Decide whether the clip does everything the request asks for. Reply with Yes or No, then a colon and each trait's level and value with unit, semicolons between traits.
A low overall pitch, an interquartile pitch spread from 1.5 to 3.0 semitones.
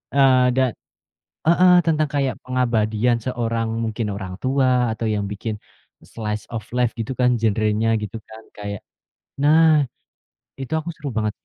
No: low, 115 Hz; average, 3.6 semitones